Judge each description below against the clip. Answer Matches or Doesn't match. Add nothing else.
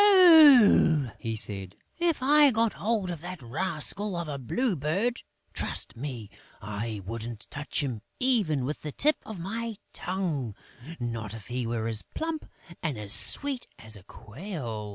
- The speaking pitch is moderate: Matches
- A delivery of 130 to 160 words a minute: Matches